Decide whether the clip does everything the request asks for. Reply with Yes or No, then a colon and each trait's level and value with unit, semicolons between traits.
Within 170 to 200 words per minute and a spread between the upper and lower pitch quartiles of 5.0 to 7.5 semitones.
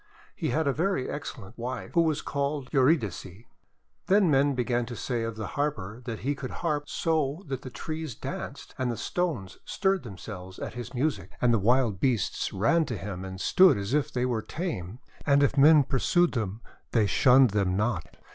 Yes: average, 190 wpm; wide, 5.4 semitones